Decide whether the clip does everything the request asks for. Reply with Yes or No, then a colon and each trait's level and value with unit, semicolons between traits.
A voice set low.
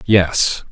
Yes: very low, 95 Hz